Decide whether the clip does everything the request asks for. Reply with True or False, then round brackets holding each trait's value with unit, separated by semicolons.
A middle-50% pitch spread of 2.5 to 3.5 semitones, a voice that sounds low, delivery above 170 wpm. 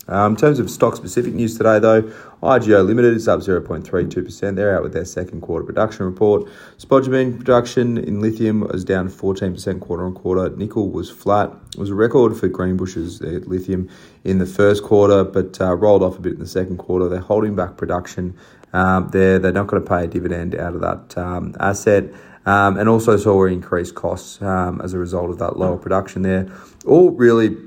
True (2.8 semitones; 95 Hz; 195 wpm)